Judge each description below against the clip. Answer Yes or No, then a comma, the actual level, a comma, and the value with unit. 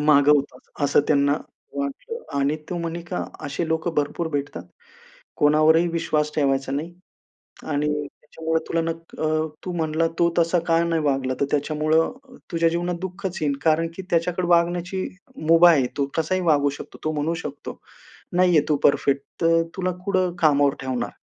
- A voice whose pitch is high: No, medium, 160 Hz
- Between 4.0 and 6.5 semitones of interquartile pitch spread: No, average, 2.7 semitones